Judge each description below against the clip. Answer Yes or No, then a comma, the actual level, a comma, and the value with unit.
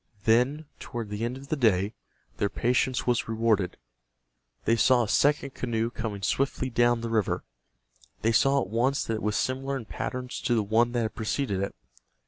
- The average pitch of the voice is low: Yes, low, 115 Hz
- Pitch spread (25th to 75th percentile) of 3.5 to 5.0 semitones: No, average, 2.8 semitones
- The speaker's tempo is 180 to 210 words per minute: Yes, average, 185 wpm